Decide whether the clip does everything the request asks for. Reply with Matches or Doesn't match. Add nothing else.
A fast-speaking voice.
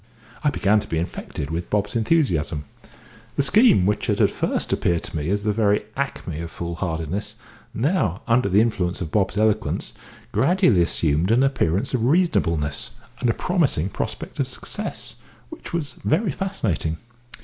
Doesn't match